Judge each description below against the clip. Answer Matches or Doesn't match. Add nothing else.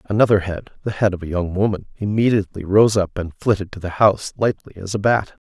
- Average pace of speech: Matches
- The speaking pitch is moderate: Doesn't match